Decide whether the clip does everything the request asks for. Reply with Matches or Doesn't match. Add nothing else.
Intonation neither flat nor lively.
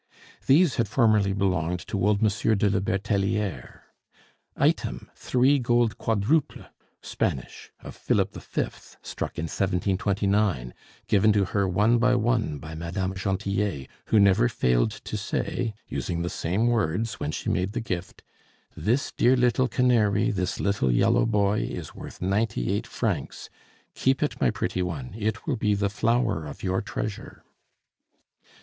Matches